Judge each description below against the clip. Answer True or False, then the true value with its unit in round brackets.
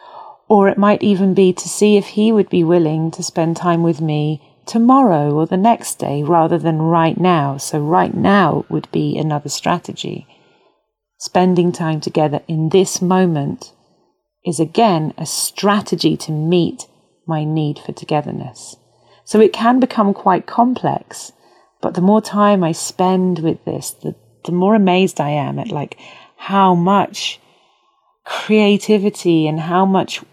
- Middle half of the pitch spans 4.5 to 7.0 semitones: False (3.9 semitones)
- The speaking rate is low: False (150 wpm)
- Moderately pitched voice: True (175 Hz)